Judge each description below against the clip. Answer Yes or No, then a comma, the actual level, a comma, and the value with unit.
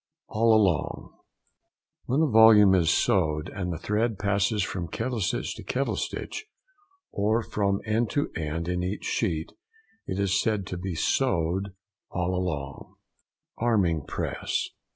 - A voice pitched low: Yes, low, 100 Hz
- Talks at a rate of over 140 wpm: No, slow, 135 wpm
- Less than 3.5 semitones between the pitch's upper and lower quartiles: No, average, 3.9 semitones